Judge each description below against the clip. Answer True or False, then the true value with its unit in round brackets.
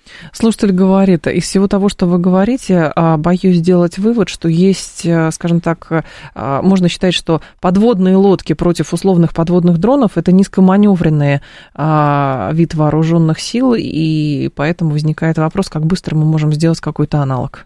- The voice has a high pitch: False (170 Hz)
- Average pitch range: True (3.2 semitones)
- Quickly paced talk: False (135 wpm)